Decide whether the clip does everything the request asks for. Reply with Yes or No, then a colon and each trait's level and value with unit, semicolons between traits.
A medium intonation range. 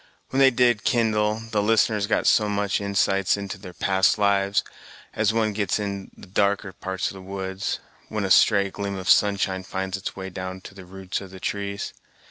No: narrow, 1.7 semitones